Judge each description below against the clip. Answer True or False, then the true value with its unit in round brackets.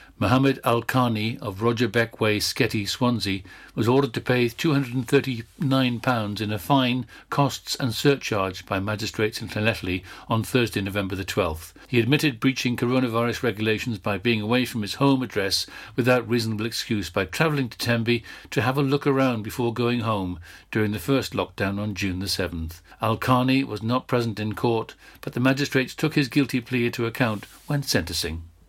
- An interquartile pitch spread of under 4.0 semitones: True (3.5 semitones)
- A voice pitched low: True (120 Hz)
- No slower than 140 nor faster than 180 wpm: True (175 wpm)